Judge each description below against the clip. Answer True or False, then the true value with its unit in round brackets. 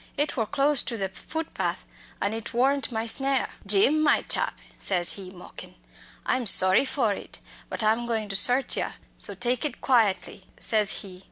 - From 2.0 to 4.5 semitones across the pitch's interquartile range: False (5.1 semitones)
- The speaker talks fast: False (175 wpm)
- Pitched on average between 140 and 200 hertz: False (225 Hz)